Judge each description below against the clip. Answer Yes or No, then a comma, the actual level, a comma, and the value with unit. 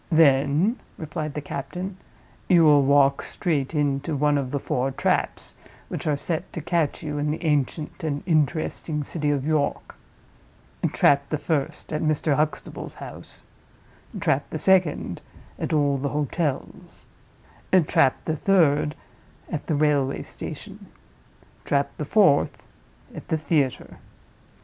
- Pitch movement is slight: Yes, narrow, 2.1 semitones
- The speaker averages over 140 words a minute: No, slow, 135 wpm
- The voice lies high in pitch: No, medium, 150 Hz